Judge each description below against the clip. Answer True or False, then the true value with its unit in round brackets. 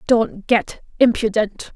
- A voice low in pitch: False (225 Hz)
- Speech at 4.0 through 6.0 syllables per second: False (3.6 syllables/s)